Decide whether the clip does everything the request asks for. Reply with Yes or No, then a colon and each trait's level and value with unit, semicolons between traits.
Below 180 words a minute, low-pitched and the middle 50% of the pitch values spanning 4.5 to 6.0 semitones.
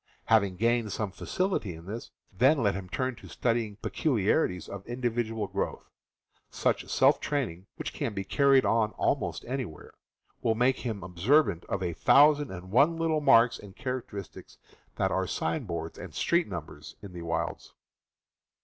Yes: average, 160 wpm; low, 110 Hz; wide, 5.5 semitones